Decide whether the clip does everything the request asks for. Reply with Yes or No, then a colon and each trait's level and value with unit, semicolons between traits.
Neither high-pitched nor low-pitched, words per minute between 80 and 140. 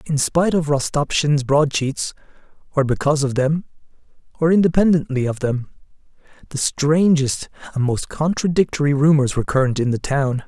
Yes: medium, 145 Hz; slow, 135 wpm